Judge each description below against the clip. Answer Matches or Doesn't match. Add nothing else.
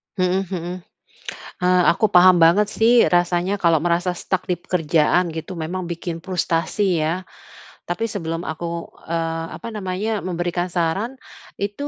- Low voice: Doesn't match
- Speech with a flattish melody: Matches